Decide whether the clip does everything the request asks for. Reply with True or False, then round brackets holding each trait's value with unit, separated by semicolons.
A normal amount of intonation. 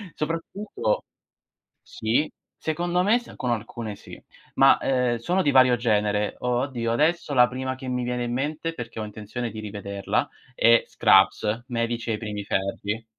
True (3.9 semitones)